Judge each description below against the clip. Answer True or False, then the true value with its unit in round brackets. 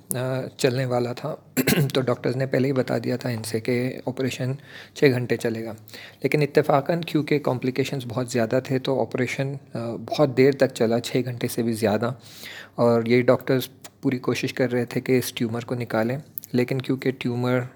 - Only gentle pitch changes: True (1.9 semitones)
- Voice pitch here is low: True (130 Hz)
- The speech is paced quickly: False (180 wpm)